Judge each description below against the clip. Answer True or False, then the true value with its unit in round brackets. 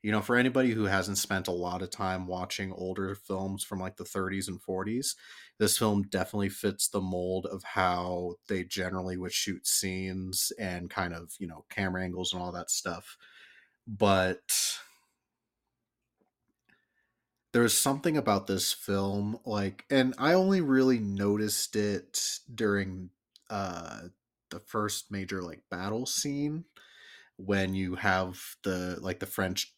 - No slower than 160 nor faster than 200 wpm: False (145 wpm)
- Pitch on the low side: True (95 Hz)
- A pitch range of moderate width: False (2.3 semitones)